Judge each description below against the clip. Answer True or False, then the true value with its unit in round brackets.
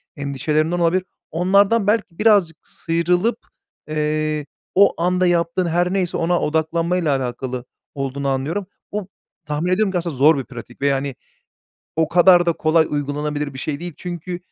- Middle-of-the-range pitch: True (165 Hz)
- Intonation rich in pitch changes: False (3.5 semitones)